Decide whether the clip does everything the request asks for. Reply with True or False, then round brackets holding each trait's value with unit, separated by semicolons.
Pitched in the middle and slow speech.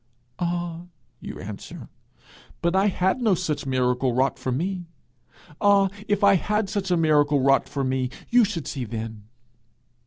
False (170 Hz; 155 wpm)